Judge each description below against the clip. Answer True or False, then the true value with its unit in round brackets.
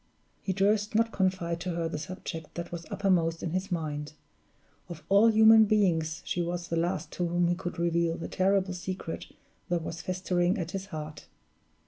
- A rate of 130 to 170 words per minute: False (180 wpm)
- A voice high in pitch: False (175 Hz)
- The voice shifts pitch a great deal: False (2.5 semitones)